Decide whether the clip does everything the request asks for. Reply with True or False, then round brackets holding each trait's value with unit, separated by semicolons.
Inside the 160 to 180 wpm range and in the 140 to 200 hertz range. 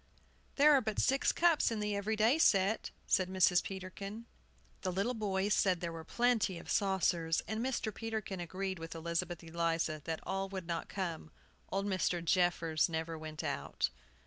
True (170 wpm; 190 Hz)